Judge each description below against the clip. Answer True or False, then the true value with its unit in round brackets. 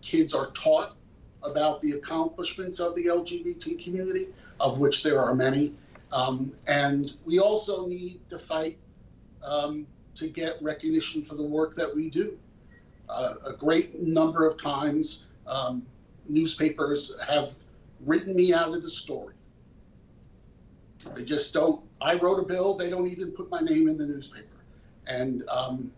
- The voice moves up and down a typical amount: True (4.0 semitones)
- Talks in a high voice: False (160 Hz)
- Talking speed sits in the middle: True (150 wpm)